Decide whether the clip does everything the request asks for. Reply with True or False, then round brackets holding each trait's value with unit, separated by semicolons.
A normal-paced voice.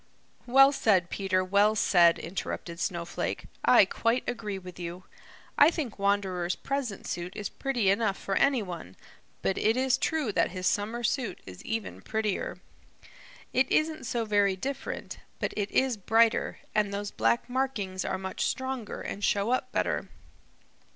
True (155 wpm)